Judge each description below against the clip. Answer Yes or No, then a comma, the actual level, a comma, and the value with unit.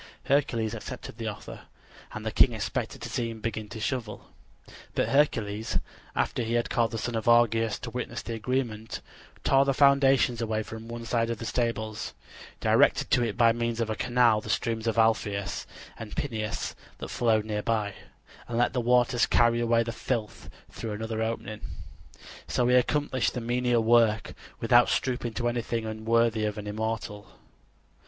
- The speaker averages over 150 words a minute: Yes, average, 175 wpm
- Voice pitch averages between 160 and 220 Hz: No, low, 115 Hz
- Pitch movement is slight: Yes, narrow, 1.6 semitones